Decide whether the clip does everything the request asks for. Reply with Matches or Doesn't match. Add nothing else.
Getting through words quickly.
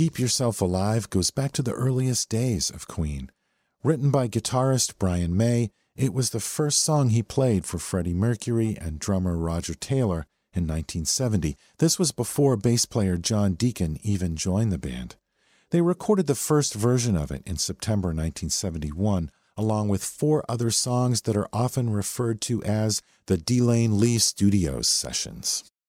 Doesn't match